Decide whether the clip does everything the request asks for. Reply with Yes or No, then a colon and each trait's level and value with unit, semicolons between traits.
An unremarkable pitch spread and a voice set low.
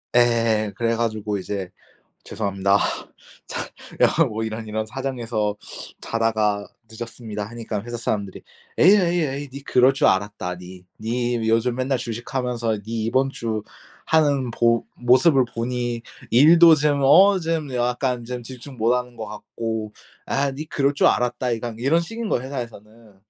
Yes: average, 3.4 semitones; low, 120 Hz